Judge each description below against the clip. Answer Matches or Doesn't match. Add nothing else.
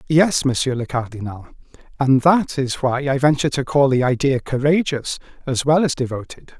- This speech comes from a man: Matches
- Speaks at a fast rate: Doesn't match